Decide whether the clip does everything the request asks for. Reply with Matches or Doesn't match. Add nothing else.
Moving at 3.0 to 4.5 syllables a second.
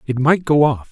Doesn't match